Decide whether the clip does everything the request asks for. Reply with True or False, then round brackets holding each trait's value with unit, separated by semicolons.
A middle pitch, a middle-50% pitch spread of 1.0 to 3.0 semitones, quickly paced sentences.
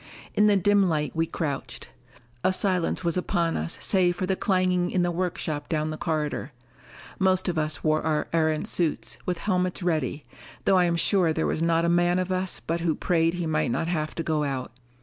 True (170 Hz; 2.7 semitones; 210 wpm)